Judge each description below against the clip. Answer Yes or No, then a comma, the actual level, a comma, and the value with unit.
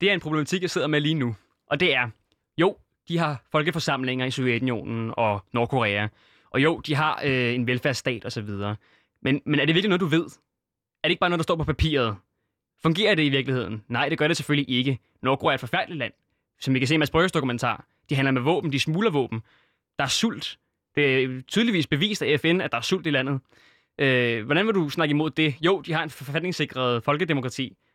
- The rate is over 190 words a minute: Yes, average, 220 wpm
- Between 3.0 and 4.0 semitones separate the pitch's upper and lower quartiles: No, average, 4.6 semitones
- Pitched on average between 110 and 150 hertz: Yes, medium, 140 Hz